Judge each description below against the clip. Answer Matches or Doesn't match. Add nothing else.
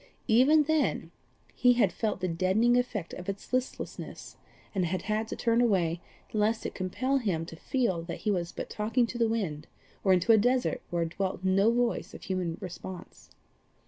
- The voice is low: Doesn't match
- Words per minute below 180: Doesn't match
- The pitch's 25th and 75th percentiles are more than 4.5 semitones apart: Matches